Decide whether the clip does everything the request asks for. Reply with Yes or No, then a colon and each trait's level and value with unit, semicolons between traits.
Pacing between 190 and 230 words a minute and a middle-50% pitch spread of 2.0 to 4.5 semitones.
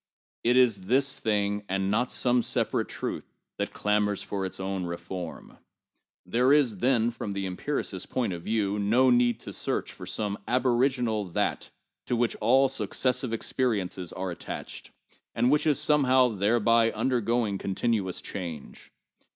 No: average, 145 wpm; average, 4.2 semitones